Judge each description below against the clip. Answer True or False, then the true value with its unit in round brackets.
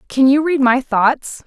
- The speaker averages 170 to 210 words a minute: True (205 wpm)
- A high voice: True (265 Hz)